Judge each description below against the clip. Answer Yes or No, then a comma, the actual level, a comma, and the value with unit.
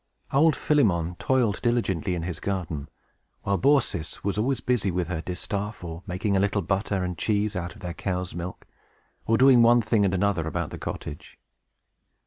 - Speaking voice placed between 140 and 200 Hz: No, low, 100 Hz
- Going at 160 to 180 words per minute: Yes, average, 170 wpm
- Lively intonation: No, average, 4.2 semitones